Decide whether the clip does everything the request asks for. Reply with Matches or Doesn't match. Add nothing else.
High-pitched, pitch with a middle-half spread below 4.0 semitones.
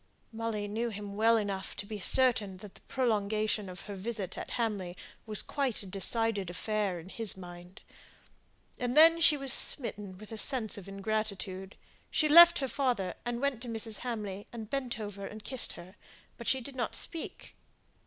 Matches